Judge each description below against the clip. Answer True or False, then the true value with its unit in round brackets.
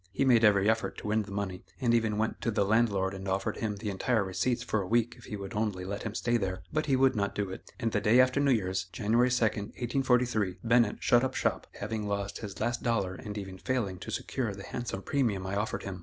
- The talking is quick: True (245 wpm)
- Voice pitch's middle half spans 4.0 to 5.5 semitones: False (3.3 semitones)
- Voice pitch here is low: True (105 Hz)